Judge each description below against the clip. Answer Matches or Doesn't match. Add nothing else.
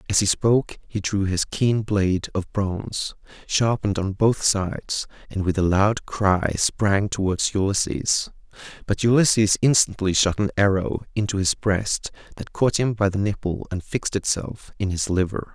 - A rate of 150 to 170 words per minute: Matches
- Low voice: Matches